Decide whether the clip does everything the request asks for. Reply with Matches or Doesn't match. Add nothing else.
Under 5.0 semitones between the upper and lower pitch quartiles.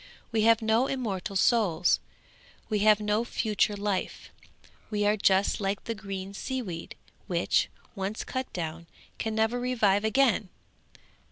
Matches